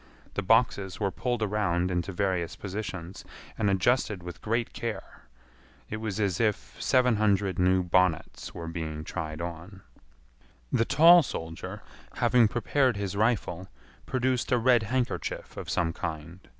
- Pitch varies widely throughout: No, average, 4.6 semitones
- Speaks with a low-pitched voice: Yes, low, 100 Hz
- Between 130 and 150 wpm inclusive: Yes, average, 140 wpm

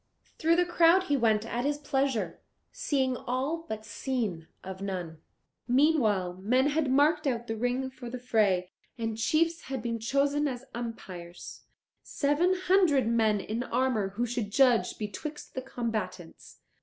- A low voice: No, high, 245 Hz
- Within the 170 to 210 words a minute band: No, average, 150 wpm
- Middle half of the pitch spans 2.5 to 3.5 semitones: No, average, 4.8 semitones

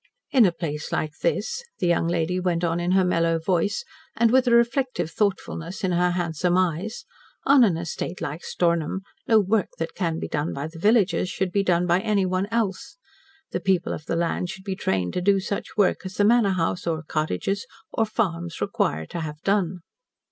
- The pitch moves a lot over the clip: No, average, 3.3 semitones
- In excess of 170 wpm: Yes, average, 200 wpm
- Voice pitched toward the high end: No, medium, 180 Hz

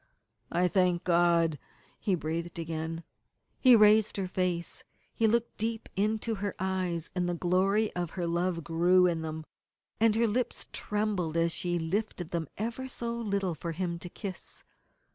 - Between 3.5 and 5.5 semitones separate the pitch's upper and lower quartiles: Yes, average, 3.8 semitones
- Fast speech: No, average, 160 wpm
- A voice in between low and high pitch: Yes, medium, 180 Hz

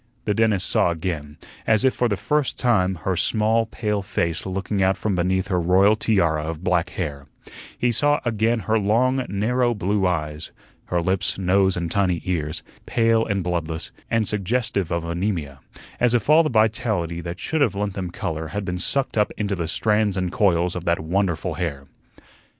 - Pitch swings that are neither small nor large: Yes, average, 4.2 semitones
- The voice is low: Yes, very low, 95 Hz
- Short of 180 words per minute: No, average, 185 wpm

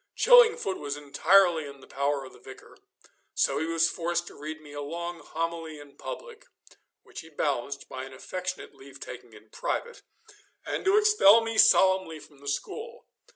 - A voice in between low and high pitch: Yes, medium, 165 Hz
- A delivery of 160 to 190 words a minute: Yes, average, 175 wpm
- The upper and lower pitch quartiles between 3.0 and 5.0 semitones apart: No, wide, 5.4 semitones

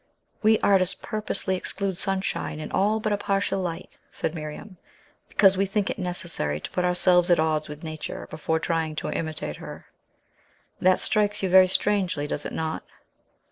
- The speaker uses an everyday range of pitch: Yes, average, 3.7 semitones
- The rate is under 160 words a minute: No, average, 170 wpm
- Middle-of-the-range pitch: Yes, medium, 180 Hz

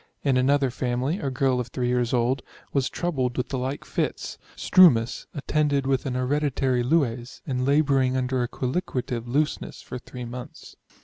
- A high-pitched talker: No, low, 130 Hz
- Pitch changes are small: Yes, narrow, 2.1 semitones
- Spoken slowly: No, average, 165 wpm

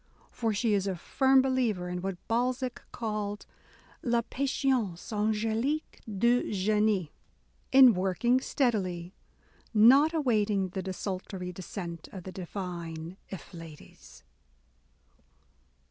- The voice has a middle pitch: No, high, 210 Hz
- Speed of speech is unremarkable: No, slow, 105 wpm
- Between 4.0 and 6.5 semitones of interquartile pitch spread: Yes, average, 4.7 semitones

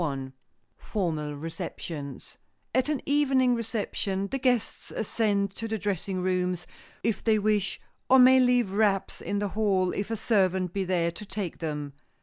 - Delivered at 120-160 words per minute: Yes, average, 155 wpm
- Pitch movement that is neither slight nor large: Yes, average, 3.9 semitones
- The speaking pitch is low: No, high, 200 Hz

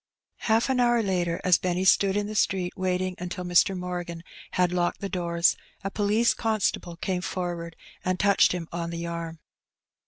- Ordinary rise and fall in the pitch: No, narrow, 2.3 semitones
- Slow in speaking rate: No, average, 175 wpm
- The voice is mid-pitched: Yes, medium, 180 Hz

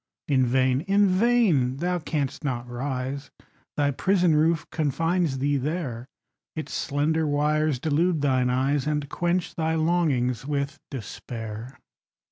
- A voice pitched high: No, medium, 145 Hz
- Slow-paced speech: Yes, slow, 125 wpm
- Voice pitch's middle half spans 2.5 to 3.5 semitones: No, average, 3.9 semitones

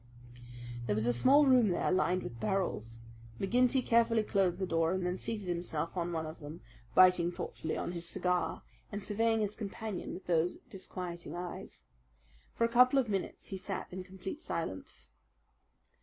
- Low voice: No, medium, 185 Hz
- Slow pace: No, average, 170 wpm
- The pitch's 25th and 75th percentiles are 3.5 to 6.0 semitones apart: Yes, average, 4.1 semitones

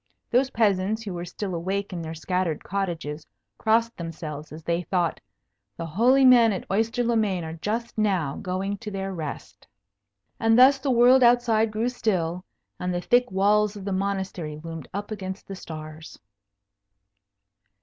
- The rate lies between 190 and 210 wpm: No, average, 160 wpm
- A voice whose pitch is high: Yes, high, 195 Hz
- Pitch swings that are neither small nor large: Yes, average, 4.9 semitones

